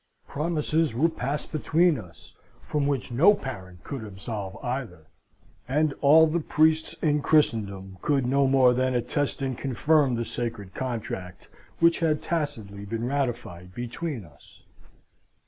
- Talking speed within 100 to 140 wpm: Yes, slow, 135 wpm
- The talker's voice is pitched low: Yes, low, 130 Hz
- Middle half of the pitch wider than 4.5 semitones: Yes, wide, 5.4 semitones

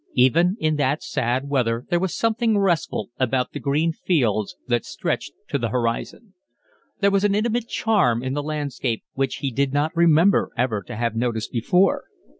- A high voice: No, medium, 140 Hz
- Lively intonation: Yes, wide, 6.7 semitones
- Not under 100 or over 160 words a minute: No, average, 175 wpm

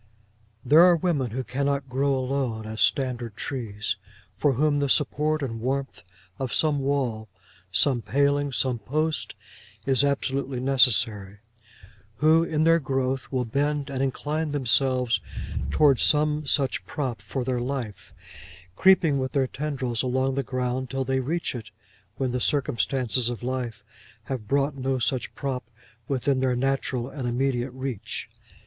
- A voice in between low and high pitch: No, low, 130 Hz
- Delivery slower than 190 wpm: Yes, average, 145 wpm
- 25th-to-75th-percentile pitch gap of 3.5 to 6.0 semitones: No, narrow, 2.4 semitones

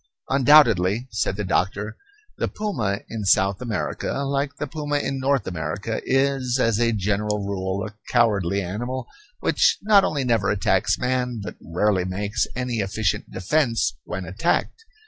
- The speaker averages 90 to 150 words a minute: Yes, average, 145 wpm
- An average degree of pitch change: Yes, average, 4.9 semitones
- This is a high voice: No, low, 110 Hz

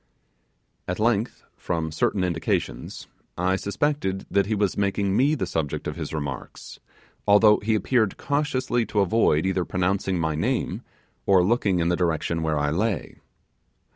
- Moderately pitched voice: No, very low, 95 Hz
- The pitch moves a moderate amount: Yes, average, 4.3 semitones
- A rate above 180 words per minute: No, average, 150 wpm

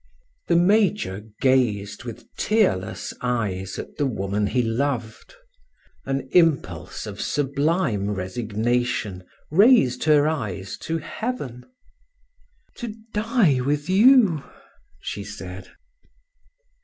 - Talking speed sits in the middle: No, slow, 95 wpm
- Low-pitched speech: Yes, low, 130 Hz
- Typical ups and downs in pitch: No, wide, 8.2 semitones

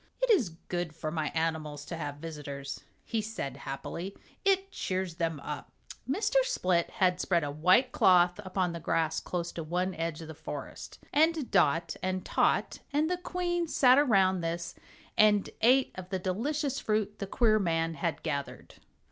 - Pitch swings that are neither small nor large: No, wide, 5.9 semitones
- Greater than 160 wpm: Yes, average, 170 wpm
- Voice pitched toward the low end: No, medium, 180 Hz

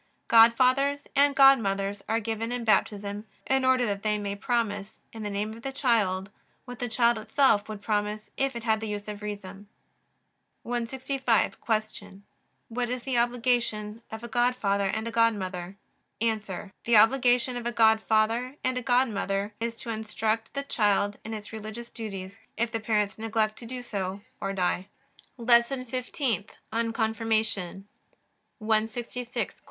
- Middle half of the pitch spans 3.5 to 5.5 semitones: No, average, 2.7 semitones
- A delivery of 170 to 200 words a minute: No, average, 155 wpm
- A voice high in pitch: Yes, high, 225 Hz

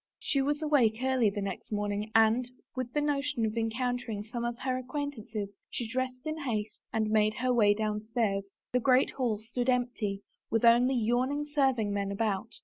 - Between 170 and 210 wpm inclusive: Yes, average, 175 wpm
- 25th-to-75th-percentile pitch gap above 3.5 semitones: No, average, 3.2 semitones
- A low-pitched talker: No, high, 235 Hz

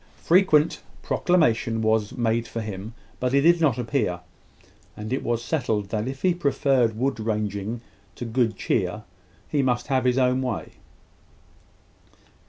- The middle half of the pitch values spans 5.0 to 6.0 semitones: No, average, 3.7 semitones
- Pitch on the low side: Yes, low, 120 Hz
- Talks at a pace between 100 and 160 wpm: Yes, average, 145 wpm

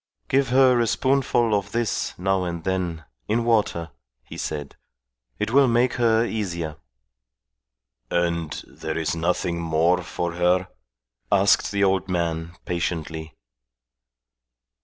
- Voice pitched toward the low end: Yes, very low, 90 Hz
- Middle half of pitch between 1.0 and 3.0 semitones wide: No, average, 5.0 semitones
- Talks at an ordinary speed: No, slow, 120 wpm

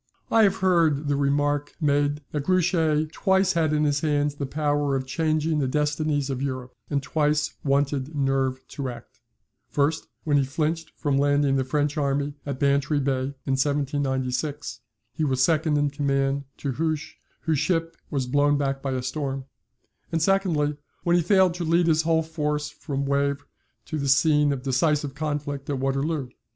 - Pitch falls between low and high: Yes, medium, 145 Hz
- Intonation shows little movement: Yes, narrow, 2.1 semitones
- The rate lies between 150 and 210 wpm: Yes, average, 170 wpm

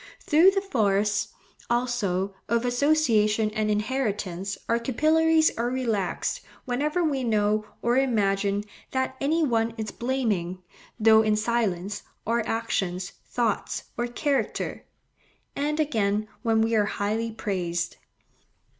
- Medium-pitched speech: No, high, 225 Hz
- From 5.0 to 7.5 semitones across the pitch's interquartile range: No, average, 4.1 semitones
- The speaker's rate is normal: No, slow, 120 wpm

